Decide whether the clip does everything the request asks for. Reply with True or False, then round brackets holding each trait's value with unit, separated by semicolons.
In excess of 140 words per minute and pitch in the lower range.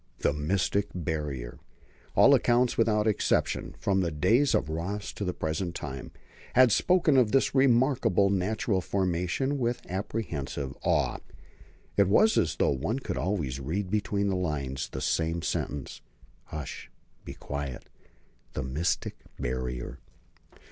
False (135 wpm; 90 Hz)